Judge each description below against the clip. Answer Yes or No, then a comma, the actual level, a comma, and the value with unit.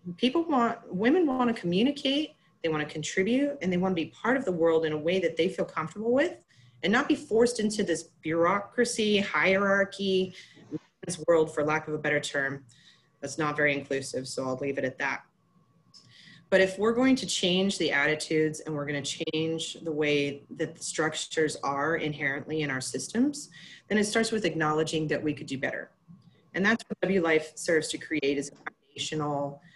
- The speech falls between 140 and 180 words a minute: No, average, 195 wpm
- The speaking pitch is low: No, medium, 165 Hz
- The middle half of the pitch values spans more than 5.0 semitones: No, average, 4.7 semitones